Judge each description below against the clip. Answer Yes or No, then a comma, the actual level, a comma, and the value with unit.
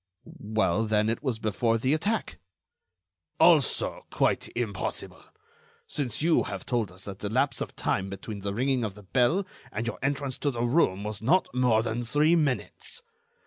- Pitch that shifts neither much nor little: Yes, average, 4.6 semitones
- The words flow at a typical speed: Yes, average, 170 wpm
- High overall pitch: No, low, 120 Hz